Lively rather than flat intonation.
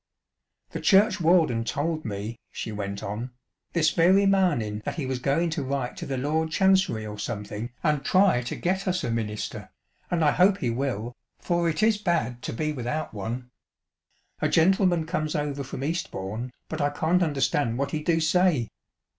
Yes: wide, 6.3 semitones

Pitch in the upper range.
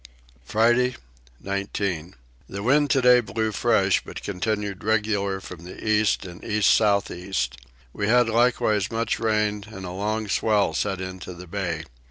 No: low, 105 Hz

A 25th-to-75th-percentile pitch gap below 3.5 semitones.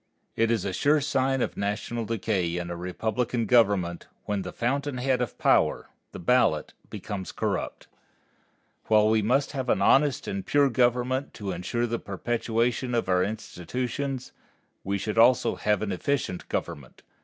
No: average, 4.3 semitones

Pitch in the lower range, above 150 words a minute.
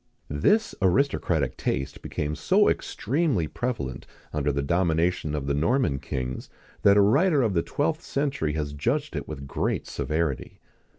No: very low, 85 Hz; average, 145 wpm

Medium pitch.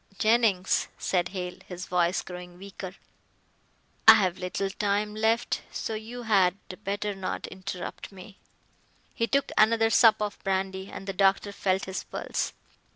No: high, 195 Hz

